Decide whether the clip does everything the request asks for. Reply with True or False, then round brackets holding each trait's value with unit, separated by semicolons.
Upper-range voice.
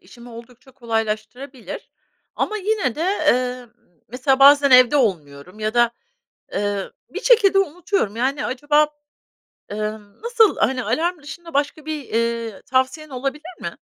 True (265 Hz)